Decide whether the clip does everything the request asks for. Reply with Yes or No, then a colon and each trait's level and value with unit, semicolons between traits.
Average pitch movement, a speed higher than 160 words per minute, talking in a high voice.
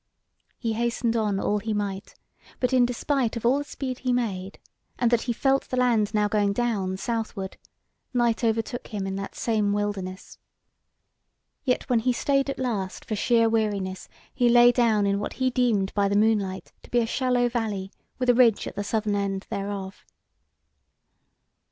Yes: average, 3.3 semitones; average, 175 wpm; high, 225 Hz